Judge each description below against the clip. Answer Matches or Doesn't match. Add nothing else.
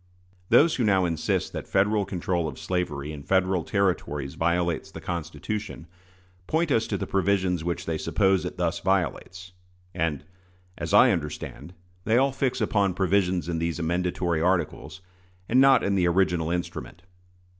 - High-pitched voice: Doesn't match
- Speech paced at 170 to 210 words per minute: Doesn't match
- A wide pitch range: Doesn't match